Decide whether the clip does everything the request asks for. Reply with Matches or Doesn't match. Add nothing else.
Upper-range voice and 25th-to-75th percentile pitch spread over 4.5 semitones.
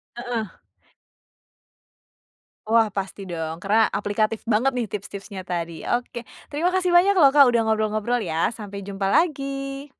Matches